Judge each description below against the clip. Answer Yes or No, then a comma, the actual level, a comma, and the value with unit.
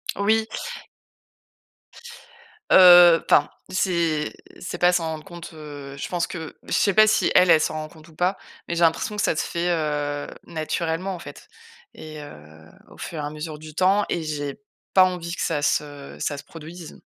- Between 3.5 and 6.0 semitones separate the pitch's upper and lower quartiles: No, average, 2.9 semitones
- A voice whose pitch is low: No, medium, 160 Hz